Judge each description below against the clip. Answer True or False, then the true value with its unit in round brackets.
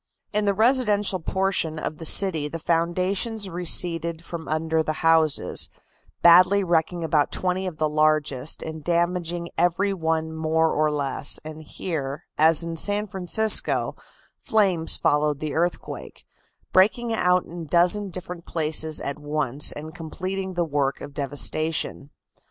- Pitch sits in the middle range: True (165 Hz)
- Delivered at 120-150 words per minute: True (140 wpm)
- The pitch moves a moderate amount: True (3.0 semitones)